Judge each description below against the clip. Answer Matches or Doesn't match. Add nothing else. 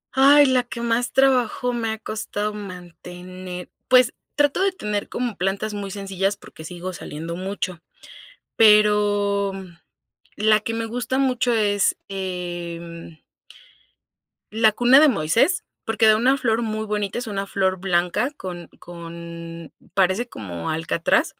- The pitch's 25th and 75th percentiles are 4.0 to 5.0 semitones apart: Matches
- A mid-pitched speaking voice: Doesn't match